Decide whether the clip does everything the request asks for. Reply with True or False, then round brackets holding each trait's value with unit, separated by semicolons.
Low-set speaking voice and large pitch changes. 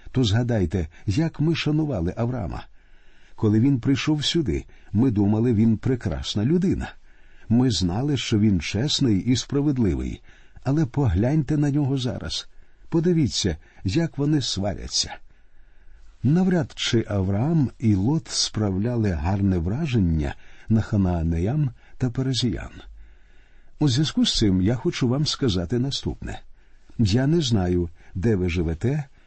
True (115 Hz; 7.1 semitones)